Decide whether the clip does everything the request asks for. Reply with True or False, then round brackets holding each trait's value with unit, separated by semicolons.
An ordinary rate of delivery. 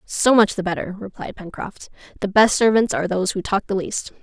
False (215 wpm)